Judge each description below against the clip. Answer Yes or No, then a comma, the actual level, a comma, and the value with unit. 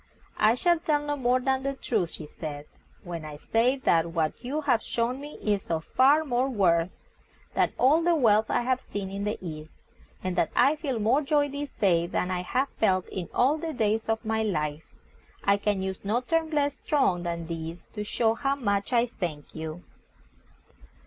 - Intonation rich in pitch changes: Yes, wide, 7.3 semitones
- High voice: Yes, high, 220 Hz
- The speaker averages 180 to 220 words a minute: Yes, average, 195 wpm